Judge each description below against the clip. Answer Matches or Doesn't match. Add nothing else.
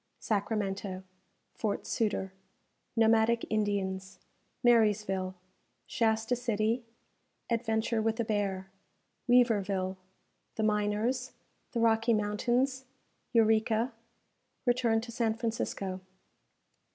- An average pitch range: Doesn't match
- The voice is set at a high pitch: Matches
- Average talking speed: Doesn't match